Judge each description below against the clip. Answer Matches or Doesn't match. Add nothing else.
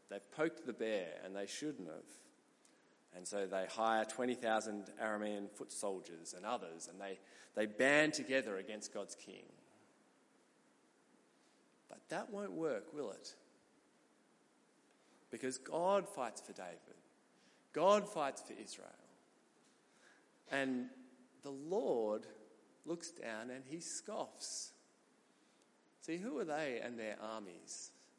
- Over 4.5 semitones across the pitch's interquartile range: Matches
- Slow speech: Matches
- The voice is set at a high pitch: Doesn't match